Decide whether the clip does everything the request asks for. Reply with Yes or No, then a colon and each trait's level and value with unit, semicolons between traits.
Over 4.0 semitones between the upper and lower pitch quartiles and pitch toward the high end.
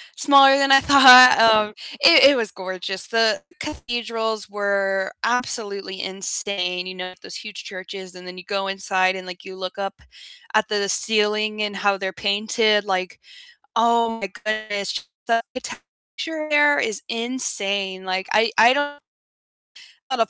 No: average, 3.3 semitones; high, 210 Hz